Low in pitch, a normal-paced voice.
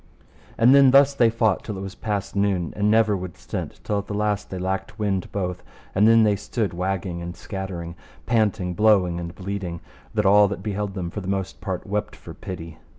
No: low, 100 Hz; fast, 210 wpm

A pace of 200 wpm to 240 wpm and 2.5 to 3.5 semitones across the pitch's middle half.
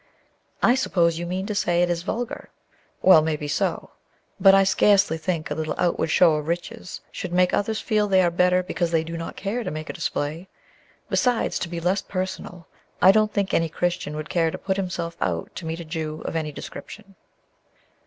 Yes: fast, 205 wpm; average, 3.1 semitones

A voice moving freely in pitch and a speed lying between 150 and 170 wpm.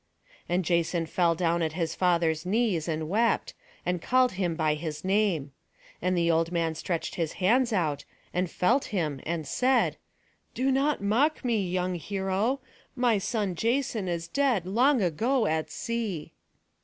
Yes: wide, 5.7 semitones; average, 155 wpm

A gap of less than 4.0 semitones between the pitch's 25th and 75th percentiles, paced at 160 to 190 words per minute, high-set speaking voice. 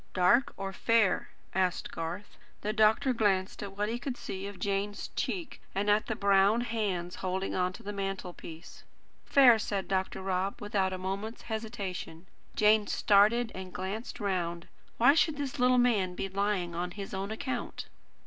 Yes: average, 2.8 semitones; average, 165 wpm; high, 200 Hz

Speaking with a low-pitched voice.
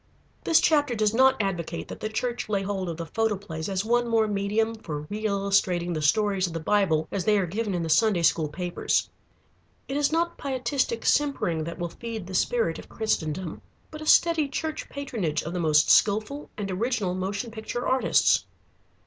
No: high, 205 Hz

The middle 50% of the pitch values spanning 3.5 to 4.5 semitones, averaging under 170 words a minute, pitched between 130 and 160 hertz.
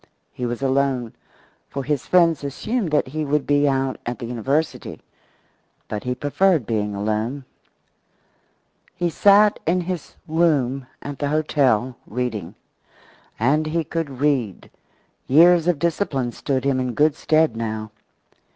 Yes: average, 4.2 semitones; slow, 135 wpm; medium, 140 Hz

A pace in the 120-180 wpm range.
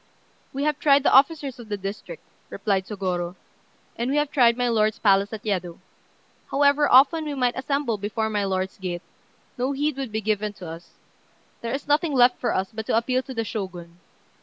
No: average, 195 wpm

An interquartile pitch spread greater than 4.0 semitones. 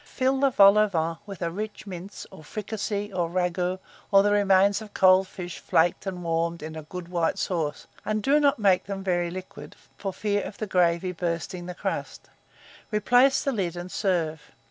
No: average, 3.1 semitones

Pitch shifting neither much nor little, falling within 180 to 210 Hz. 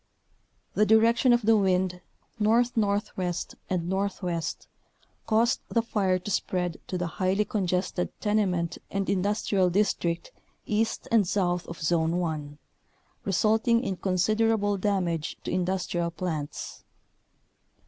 Yes: average, 3.2 semitones; high, 190 Hz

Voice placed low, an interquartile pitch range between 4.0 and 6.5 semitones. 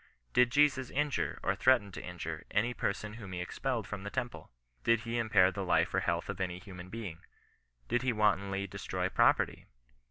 Yes: low, 105 Hz; average, 4.4 semitones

